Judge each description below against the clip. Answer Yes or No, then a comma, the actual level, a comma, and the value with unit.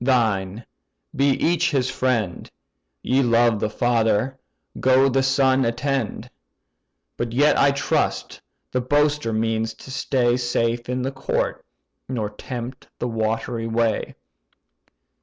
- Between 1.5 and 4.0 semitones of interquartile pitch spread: Yes, average, 2.8 semitones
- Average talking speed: No, slow, 120 wpm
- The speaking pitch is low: Yes, low, 120 Hz